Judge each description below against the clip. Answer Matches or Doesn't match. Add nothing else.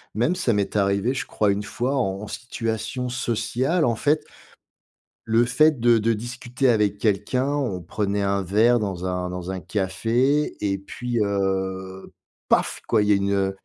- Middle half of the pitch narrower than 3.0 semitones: Doesn't match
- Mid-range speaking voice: Doesn't match